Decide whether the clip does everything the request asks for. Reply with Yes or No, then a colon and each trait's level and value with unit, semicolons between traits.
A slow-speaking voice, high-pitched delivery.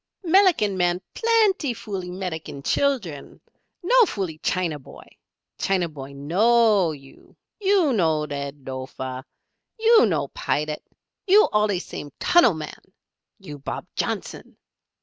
No: slow, 115 wpm; medium, 180 Hz